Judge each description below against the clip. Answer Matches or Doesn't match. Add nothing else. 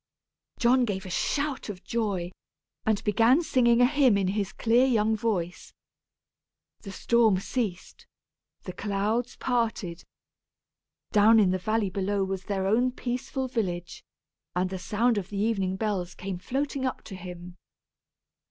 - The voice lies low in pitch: Doesn't match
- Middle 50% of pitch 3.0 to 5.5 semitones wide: Matches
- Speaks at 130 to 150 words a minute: Matches